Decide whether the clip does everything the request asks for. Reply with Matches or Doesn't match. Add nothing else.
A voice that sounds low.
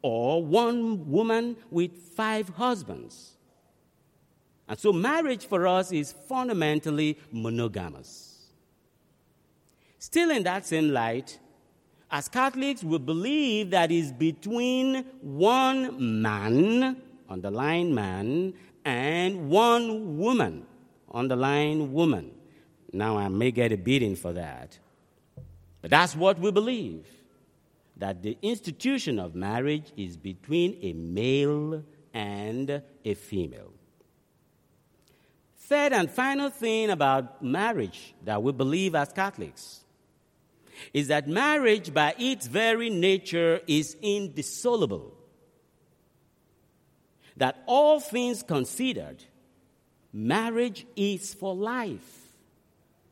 Doesn't match